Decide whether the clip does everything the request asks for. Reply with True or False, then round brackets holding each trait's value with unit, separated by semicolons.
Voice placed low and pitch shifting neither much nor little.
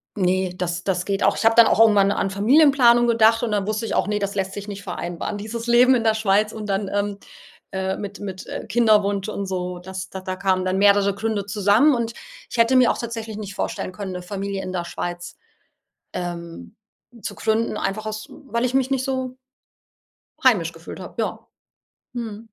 False (205 Hz; 3.1 semitones)